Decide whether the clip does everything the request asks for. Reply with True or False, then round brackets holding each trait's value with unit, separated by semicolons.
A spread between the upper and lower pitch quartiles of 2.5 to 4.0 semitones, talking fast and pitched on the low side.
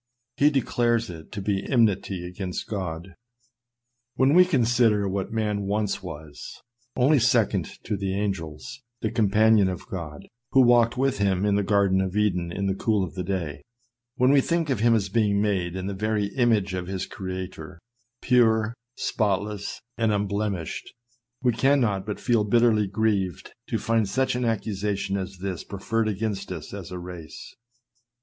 False (3.2 semitones; 165 wpm; 100 Hz)